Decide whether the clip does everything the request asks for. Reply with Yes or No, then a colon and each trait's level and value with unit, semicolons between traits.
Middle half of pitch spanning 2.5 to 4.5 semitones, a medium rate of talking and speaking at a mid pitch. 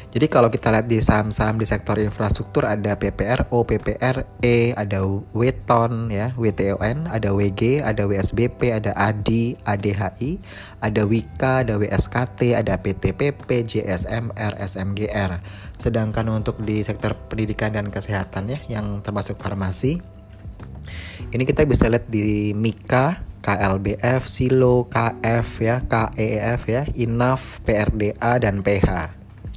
No: average, 2.8 semitones; average, 120 wpm; low, 105 Hz